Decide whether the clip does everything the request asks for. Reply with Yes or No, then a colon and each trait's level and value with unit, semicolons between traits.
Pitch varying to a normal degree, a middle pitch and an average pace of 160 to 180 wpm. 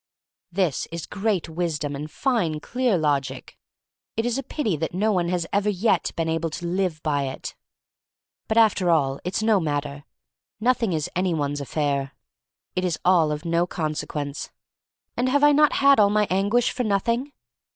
No: wide, 6.1 semitones; medium, 175 Hz; average, 175 wpm